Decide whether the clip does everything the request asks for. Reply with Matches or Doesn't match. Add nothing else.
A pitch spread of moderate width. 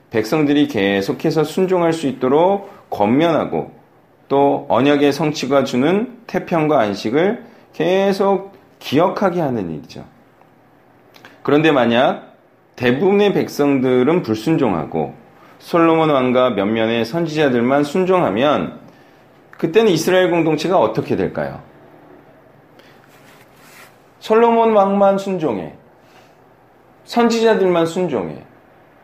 Doesn't match